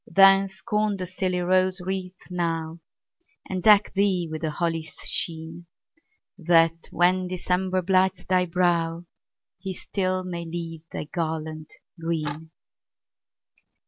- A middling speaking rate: No, slow, 115 wpm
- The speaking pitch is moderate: Yes, medium, 180 Hz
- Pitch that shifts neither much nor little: No, narrow, 2.1 semitones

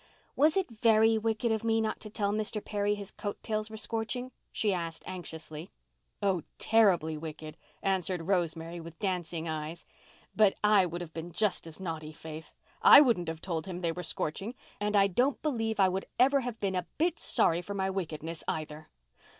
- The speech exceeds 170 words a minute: Yes, average, 180 wpm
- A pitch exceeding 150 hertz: Yes, high, 190 Hz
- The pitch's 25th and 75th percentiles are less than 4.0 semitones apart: No, average, 4.8 semitones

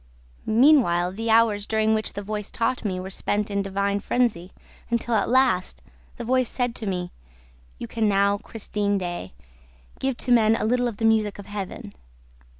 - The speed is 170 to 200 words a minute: Yes, average, 180 wpm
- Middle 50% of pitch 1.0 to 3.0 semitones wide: Yes, narrow, 2.6 semitones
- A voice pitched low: No, high, 215 Hz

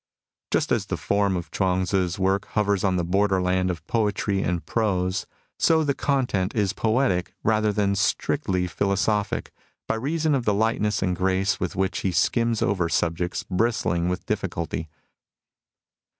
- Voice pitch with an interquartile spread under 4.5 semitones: Yes, average, 2.8 semitones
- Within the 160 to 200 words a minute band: No, average, 150 wpm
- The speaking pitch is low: Yes, very low, 95 Hz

